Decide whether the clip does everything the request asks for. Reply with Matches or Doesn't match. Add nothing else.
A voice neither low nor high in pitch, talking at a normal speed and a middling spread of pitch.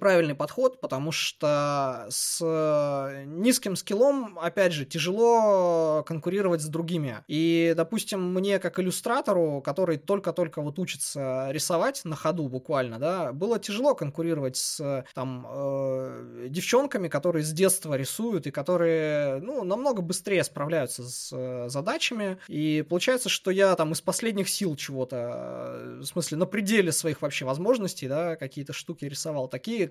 Matches